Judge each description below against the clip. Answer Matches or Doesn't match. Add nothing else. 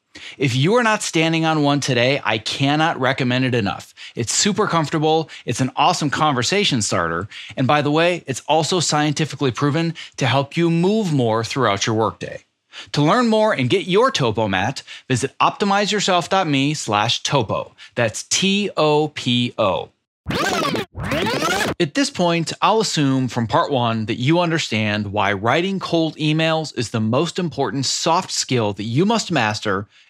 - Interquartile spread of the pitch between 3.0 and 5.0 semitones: Doesn't match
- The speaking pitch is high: Doesn't match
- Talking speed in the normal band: Matches